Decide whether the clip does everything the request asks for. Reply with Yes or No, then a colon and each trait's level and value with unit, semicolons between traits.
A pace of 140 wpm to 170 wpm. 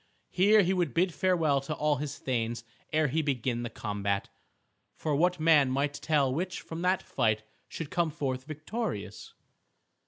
Yes: average, 160 wpm